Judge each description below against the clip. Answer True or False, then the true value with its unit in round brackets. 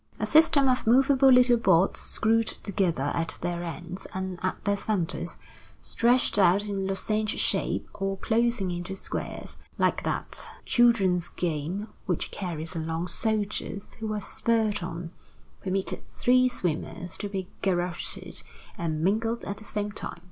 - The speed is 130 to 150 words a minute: True (140 wpm)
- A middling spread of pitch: True (4.2 semitones)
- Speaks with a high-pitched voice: True (195 Hz)